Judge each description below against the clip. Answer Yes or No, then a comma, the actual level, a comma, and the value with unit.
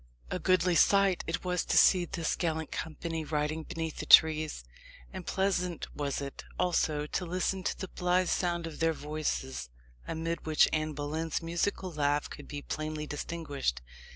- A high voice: No, medium, 160 Hz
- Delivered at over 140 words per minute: Yes, average, 160 wpm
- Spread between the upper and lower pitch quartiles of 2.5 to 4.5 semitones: Yes, average, 2.8 semitones